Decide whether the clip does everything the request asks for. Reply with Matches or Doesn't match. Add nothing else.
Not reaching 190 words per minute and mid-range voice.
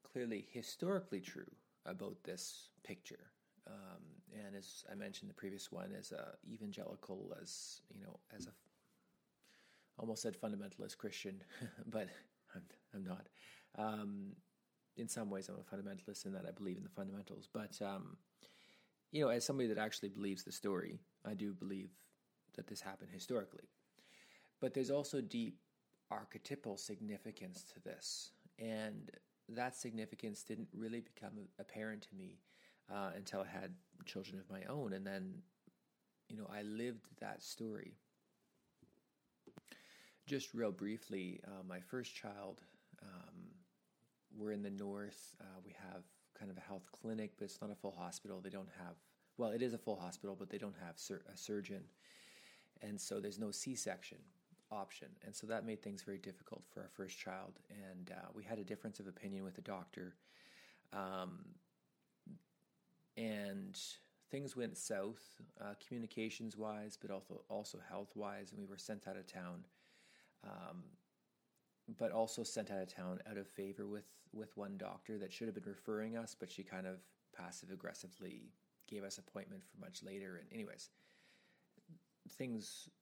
Doesn't match